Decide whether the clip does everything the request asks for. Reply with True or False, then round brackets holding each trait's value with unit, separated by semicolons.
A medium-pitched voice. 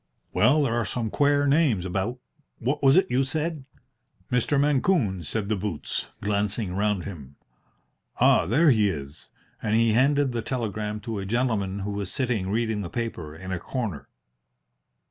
False (110 Hz)